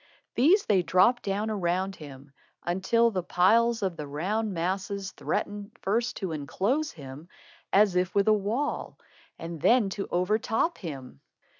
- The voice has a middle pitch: No, high, 195 Hz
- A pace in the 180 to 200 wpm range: No, average, 140 wpm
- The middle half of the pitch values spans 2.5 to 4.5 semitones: Yes, average, 4.2 semitones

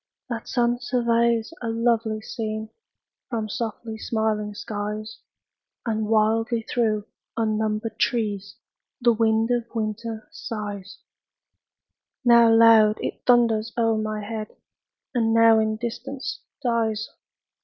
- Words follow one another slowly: Yes, slow, 110 wpm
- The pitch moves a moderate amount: No, narrow, 1.4 semitones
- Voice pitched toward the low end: No, high, 225 Hz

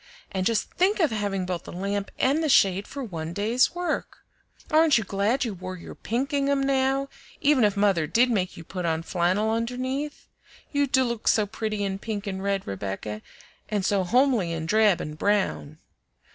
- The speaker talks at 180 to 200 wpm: Yes, average, 185 wpm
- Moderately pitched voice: No, high, 210 Hz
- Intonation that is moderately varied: No, wide, 5.8 semitones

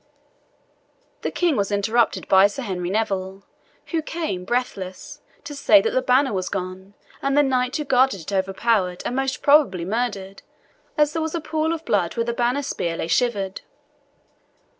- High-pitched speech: Yes, high, 235 Hz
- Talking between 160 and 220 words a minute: Yes, average, 170 wpm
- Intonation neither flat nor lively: No, wide, 6.9 semitones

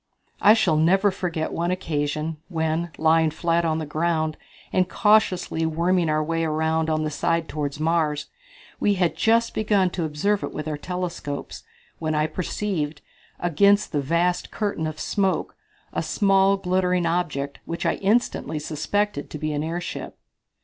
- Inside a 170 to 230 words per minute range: No, average, 155 wpm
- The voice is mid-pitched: Yes, medium, 165 Hz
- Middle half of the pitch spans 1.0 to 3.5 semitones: Yes, average, 3.0 semitones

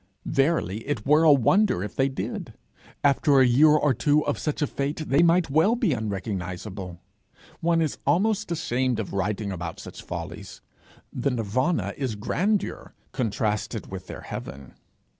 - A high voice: No, low, 135 Hz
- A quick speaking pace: No, average, 155 wpm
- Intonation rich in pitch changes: Yes, wide, 7.0 semitones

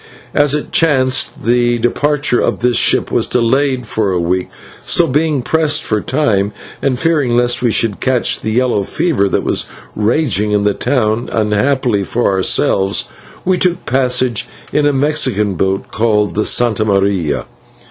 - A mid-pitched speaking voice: No, low, 120 Hz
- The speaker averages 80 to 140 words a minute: No, average, 160 wpm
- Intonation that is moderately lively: Yes, average, 4.8 semitones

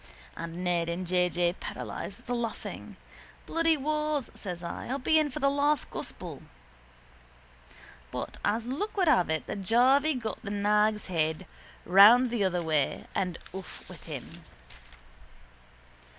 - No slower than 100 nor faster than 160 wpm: Yes, average, 150 wpm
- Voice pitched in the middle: No, high, 210 Hz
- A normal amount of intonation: No, wide, 7.5 semitones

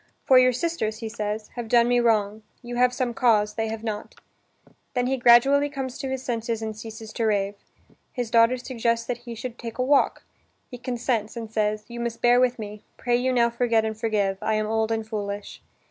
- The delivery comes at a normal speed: No, fast, 210 wpm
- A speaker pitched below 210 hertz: No, high, 230 Hz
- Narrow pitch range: Yes, narrow, 2.2 semitones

